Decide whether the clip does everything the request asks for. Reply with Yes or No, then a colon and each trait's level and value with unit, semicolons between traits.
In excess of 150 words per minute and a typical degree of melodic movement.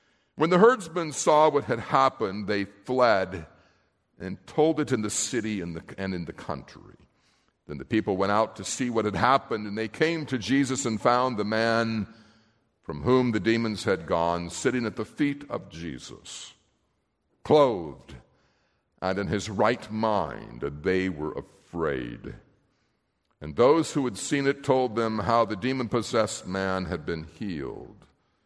Yes: average, 160 wpm; average, 4.9 semitones